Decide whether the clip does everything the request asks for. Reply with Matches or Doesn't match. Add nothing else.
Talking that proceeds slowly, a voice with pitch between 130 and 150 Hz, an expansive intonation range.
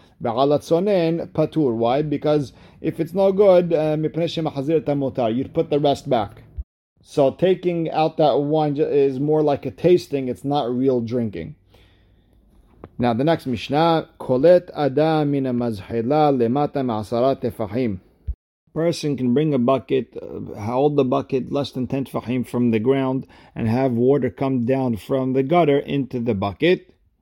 Doesn't match